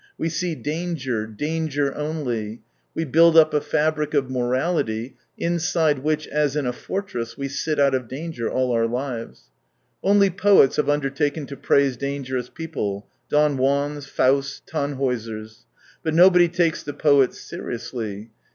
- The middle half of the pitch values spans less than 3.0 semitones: No, average, 4.0 semitones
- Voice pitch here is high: No, medium, 140 Hz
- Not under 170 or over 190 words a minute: No, average, 145 wpm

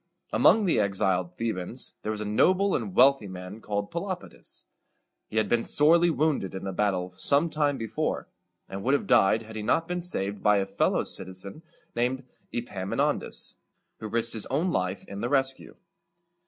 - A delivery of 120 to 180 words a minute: No, average, 190 wpm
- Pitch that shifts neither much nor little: No, wide, 6.6 semitones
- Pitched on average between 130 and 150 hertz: No, low, 110 Hz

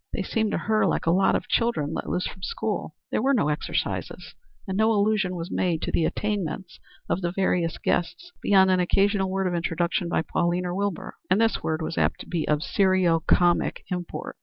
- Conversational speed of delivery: No, fast, 210 wpm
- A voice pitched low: No, medium, 185 Hz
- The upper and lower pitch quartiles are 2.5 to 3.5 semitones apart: Yes, average, 2.9 semitones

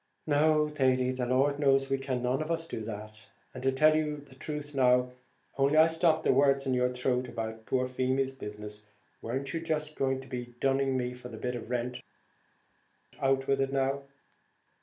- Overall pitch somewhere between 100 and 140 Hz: Yes, low, 135 Hz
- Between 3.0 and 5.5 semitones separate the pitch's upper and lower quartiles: No, narrow, 2.4 semitones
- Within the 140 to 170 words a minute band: No, average, 185 wpm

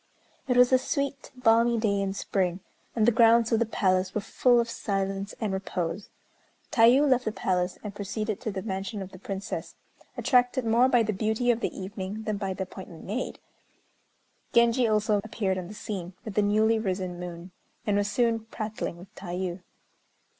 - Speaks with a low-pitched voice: No, high, 210 Hz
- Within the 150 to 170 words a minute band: No, average, 180 wpm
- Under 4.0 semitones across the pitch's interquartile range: Yes, average, 3.4 semitones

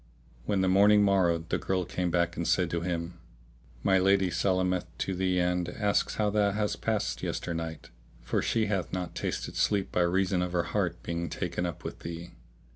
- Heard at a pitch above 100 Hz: No, very low, 90 Hz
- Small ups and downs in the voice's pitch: Yes, narrow, 2.2 semitones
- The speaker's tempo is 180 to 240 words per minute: Yes, average, 190 wpm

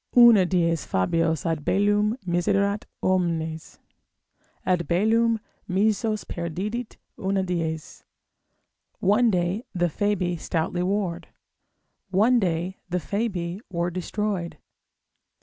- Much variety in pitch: No, average, 3.3 semitones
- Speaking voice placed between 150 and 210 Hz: Yes, medium, 185 Hz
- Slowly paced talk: Yes, slow, 95 wpm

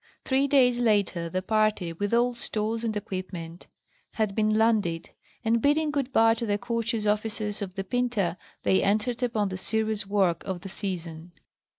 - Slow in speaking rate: No, average, 170 wpm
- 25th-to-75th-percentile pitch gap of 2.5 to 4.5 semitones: Yes, average, 3.5 semitones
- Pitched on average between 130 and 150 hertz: No, high, 215 Hz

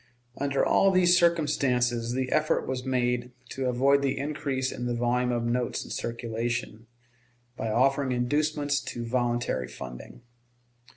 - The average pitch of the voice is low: Yes, low, 125 Hz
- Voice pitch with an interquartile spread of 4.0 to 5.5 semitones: No, average, 2.7 semitones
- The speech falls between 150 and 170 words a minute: No, slow, 135 wpm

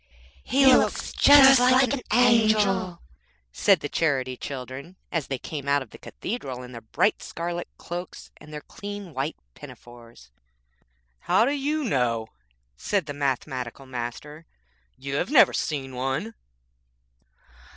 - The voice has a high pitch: No, medium, 150 Hz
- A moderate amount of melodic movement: No, wide, 8.6 semitones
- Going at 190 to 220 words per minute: No, slow, 135 wpm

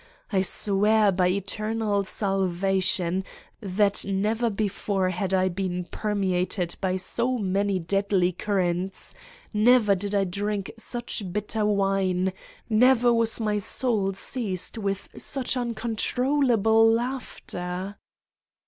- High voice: Yes, high, 200 Hz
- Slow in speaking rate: Yes, slow, 110 wpm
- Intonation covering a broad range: No, average, 2.8 semitones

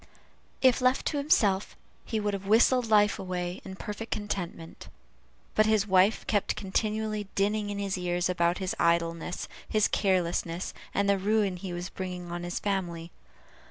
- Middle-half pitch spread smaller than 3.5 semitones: Yes, average, 3.0 semitones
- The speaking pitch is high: Yes, high, 195 Hz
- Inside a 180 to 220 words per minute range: No, average, 160 wpm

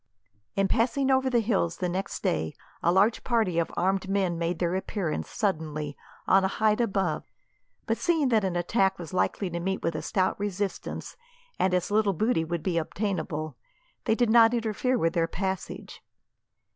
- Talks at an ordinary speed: Yes, average, 175 wpm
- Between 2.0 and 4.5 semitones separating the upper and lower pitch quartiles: Yes, average, 4.1 semitones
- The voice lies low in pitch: No, high, 190 Hz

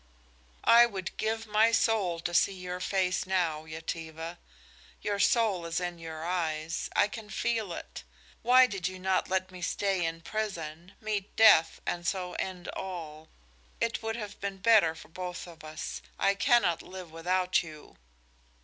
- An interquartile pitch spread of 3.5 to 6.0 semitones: Yes, average, 4.0 semitones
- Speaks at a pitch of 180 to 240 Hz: Yes, medium, 185 Hz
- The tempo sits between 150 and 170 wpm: Yes, average, 160 wpm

